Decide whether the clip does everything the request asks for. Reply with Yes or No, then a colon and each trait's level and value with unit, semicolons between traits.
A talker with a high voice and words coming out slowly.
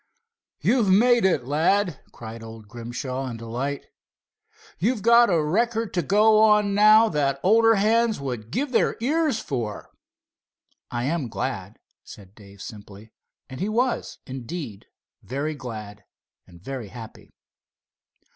No: medium, 150 Hz; slow, 130 wpm